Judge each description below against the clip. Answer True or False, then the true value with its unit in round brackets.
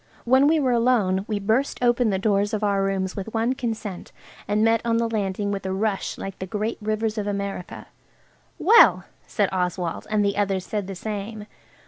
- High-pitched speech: True (210 Hz)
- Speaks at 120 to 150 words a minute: False (190 wpm)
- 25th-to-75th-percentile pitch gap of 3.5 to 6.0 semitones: False (2.7 semitones)